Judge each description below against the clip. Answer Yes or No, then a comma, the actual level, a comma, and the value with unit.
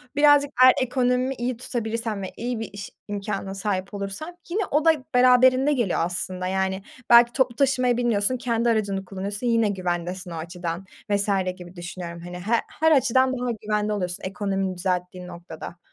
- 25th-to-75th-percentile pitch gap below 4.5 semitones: No, average, 5.1 semitones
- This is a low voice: No, high, 205 Hz